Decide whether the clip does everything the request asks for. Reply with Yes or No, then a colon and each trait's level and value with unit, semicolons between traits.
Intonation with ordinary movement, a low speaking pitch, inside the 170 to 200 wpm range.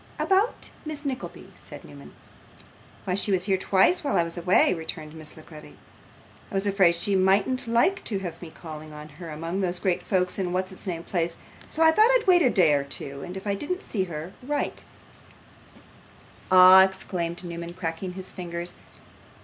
No: average, 3.2 semitones; medium, 185 Hz; average, 190 wpm